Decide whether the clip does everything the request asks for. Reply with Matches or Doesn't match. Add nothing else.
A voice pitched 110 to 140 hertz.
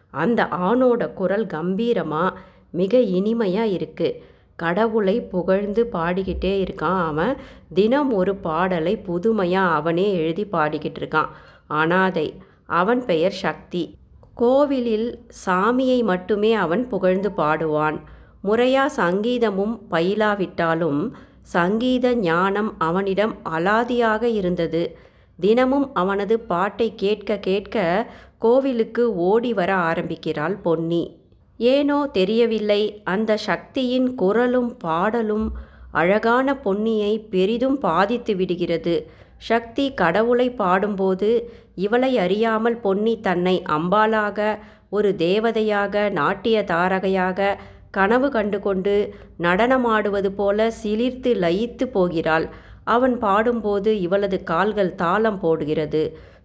Doesn't match